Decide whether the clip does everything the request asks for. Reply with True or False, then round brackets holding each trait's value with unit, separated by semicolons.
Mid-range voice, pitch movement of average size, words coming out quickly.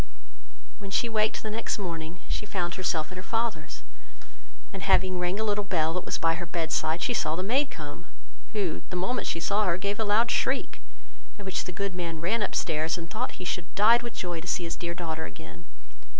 True (180 Hz; 3.7 semitones; 225 wpm)